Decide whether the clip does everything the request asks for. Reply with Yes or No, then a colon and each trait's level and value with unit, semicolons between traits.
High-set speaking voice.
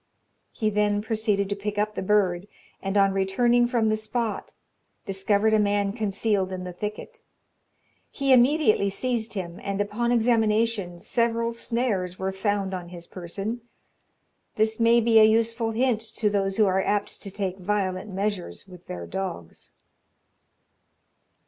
Yes: high, 210 Hz